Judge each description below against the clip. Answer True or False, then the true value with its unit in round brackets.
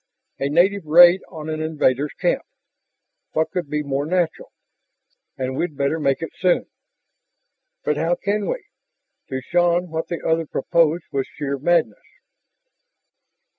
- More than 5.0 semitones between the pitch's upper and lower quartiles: False (3.4 semitones)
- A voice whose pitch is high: False (160 Hz)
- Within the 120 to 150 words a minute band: True (135 wpm)